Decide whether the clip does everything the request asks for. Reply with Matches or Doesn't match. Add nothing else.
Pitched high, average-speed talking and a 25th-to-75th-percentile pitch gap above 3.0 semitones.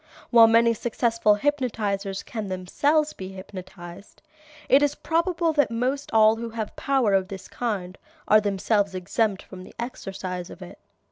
Matches